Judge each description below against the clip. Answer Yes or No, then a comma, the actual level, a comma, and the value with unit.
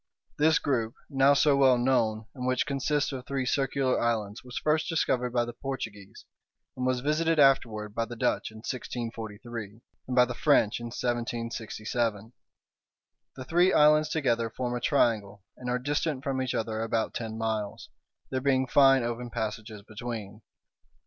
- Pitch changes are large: No, average, 3.2 semitones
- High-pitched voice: No, low, 125 Hz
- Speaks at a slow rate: No, average, 160 wpm